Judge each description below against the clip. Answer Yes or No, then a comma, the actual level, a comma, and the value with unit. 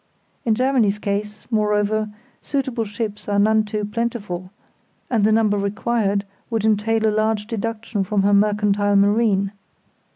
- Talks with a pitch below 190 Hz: No, high, 210 Hz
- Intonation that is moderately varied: No, narrow, 1.7 semitones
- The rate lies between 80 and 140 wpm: Yes, slow, 135 wpm